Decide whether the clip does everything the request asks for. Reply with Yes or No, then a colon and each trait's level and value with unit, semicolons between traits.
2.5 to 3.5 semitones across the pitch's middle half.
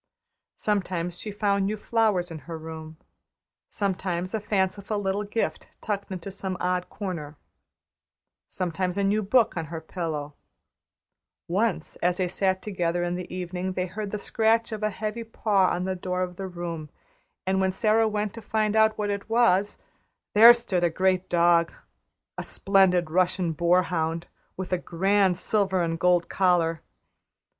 Yes: average, 2.9 semitones